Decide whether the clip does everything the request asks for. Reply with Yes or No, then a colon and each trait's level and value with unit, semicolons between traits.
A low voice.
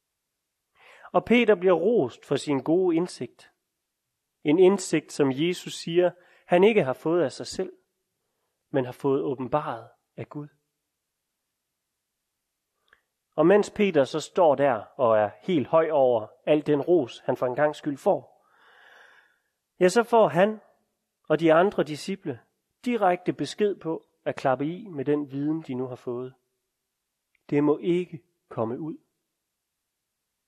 No: medium, 155 Hz